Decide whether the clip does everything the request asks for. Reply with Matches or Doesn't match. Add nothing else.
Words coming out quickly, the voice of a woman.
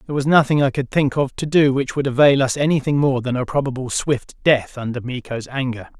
Doesn't match